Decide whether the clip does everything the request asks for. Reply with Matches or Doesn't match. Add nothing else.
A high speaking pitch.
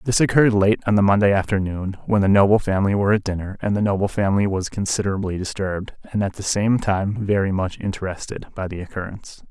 Doesn't match